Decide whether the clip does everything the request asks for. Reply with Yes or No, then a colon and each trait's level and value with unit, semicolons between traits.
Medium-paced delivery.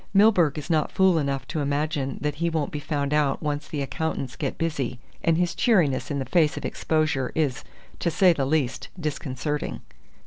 Yes: average, 180 wpm